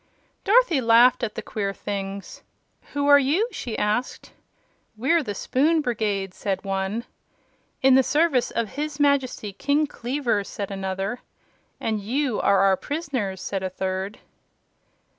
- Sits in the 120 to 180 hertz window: No, high, 230 Hz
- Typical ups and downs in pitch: No, wide, 6.3 semitones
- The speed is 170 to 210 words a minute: No, average, 140 wpm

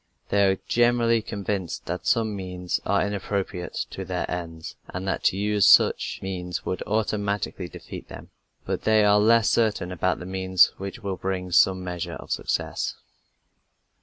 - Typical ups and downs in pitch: No, narrow, 2.3 semitones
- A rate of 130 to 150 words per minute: No, average, 160 wpm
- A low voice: Yes, very low, 95 Hz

